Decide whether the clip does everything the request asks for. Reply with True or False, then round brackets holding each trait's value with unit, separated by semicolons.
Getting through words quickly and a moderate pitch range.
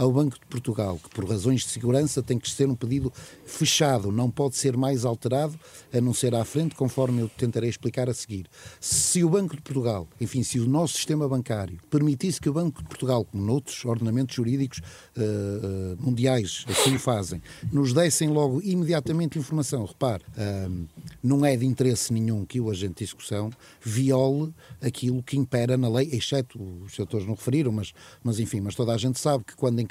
True (195 wpm; 3.7 semitones)